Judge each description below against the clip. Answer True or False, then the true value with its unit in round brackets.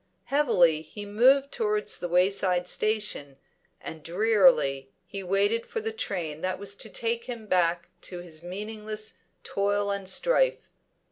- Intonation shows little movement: False (4.4 semitones)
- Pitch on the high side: True (200 Hz)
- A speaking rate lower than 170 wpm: True (140 wpm)